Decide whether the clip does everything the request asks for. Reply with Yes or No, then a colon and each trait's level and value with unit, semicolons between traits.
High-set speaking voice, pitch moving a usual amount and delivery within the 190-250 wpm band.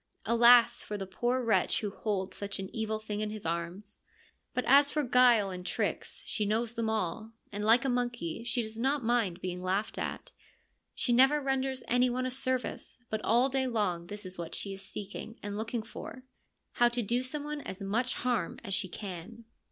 Yes: high, 225 Hz; average, 3.7 semitones; average, 200 wpm